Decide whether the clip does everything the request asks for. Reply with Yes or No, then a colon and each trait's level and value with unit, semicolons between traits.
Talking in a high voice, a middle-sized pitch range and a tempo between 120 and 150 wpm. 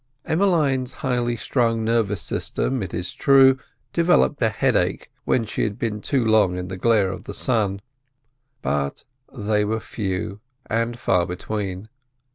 No: low, 110 Hz; average, 4.2 semitones; average, 145 wpm